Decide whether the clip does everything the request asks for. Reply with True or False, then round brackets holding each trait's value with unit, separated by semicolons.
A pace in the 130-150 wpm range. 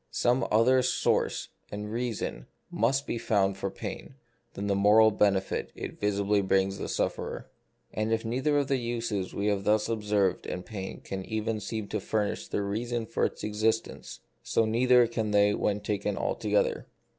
False (170 wpm)